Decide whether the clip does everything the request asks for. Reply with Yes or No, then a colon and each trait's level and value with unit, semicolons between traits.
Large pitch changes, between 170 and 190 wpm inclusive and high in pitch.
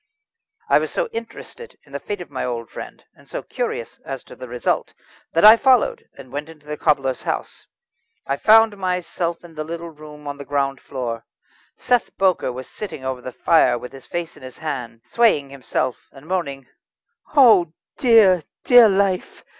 No: wide, 7.2 semitones; average, 180 wpm; medium, 160 Hz